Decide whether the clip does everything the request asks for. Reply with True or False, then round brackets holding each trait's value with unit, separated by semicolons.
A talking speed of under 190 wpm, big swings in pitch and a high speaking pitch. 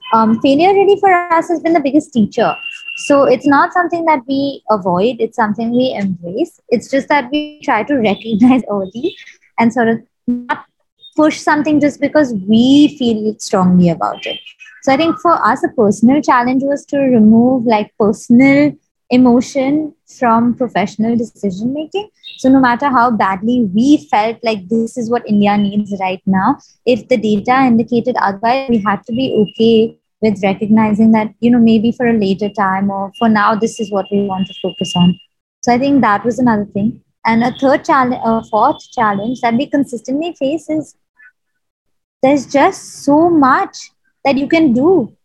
False (175 wpm; 4.7 semitones; 245 Hz)